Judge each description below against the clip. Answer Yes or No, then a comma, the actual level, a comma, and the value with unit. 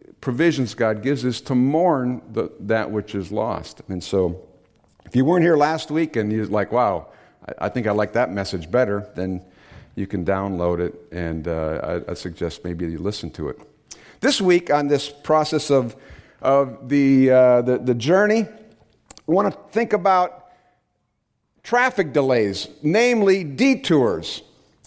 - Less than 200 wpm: Yes, average, 160 wpm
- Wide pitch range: Yes, wide, 7.5 semitones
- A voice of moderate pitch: No, low, 125 Hz